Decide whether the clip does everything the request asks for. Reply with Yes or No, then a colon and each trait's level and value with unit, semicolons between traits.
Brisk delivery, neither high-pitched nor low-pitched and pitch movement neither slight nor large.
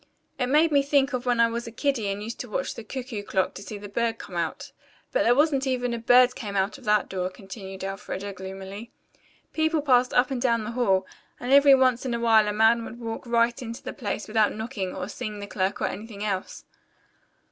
No: fast, 230 wpm; high, 230 Hz; average, 3.7 semitones